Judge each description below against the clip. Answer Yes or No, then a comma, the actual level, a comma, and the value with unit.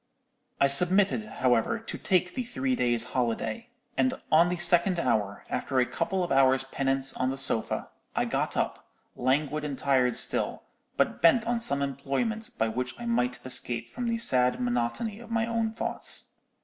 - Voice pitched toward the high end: No, medium, 140 Hz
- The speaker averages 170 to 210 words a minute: Yes, average, 175 wpm